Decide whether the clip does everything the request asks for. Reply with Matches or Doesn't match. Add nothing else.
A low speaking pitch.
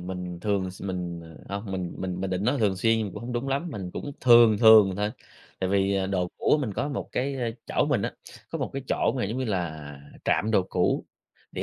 Matches